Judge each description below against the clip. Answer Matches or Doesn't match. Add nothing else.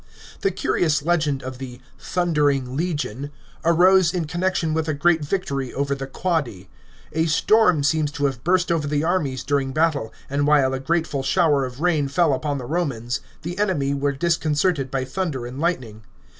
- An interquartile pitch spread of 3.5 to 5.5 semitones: Matches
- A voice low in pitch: Doesn't match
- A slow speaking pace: Doesn't match